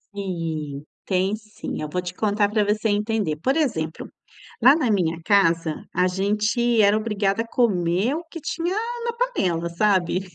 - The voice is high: Yes, high, 205 Hz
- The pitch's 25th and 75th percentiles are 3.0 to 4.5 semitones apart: Yes, average, 4.1 semitones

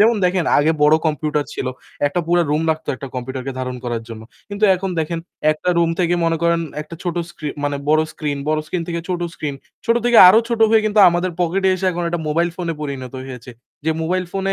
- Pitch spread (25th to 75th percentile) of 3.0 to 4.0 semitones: Yes, average, 3.7 semitones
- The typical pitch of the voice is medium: Yes, medium, 165 Hz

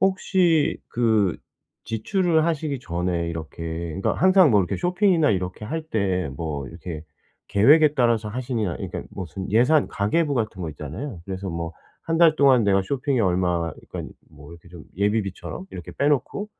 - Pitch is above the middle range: No, low, 105 Hz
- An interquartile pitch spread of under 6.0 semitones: No, wide, 9.0 semitones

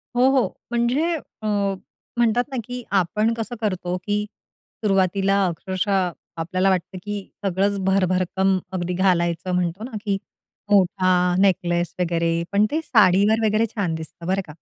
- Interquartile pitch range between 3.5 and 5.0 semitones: No, average, 2.9 semitones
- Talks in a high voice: Yes, high, 195 Hz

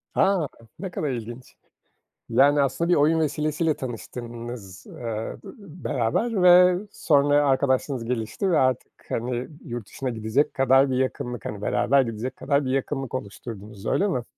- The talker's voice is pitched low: Yes, low, 130 Hz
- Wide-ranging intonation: No, average, 3.9 semitones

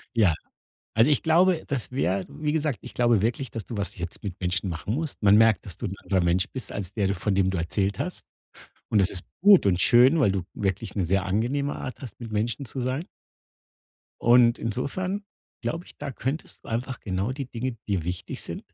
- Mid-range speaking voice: No, low, 115 Hz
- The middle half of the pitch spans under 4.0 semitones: No, wide, 5.5 semitones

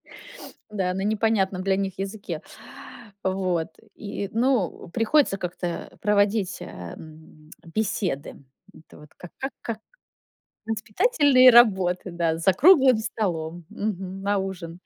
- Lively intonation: No, average, 3.7 semitones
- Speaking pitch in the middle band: No, high, 195 Hz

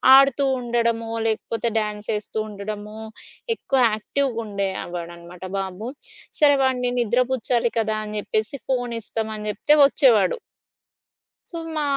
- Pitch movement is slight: No, average, 3.0 semitones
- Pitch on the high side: Yes, high, 220 Hz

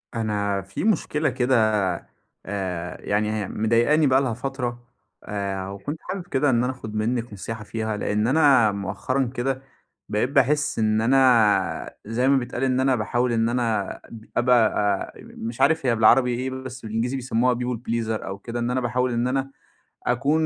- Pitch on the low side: Yes, low, 120 Hz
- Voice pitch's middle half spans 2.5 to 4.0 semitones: Yes, average, 3.3 semitones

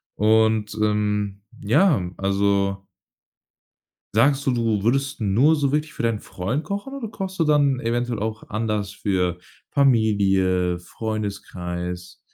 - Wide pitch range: Yes, wide, 5.7 semitones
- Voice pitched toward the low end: Yes, low, 110 Hz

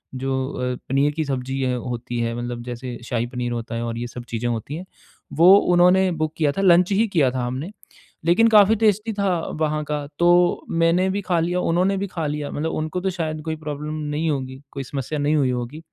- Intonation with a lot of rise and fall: Yes, wide, 5.7 semitones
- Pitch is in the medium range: Yes, medium, 150 Hz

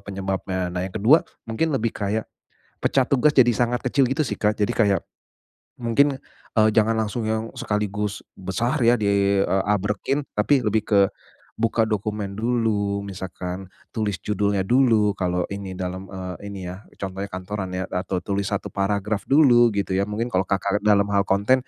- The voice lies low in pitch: Yes, low, 105 Hz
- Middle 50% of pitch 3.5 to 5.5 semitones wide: No, average, 2.9 semitones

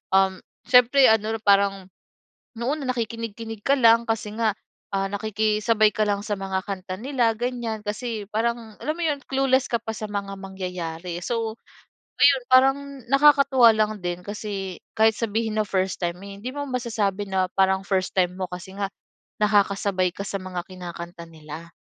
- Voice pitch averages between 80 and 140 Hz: No, high, 210 Hz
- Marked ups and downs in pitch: No, average, 3.4 semitones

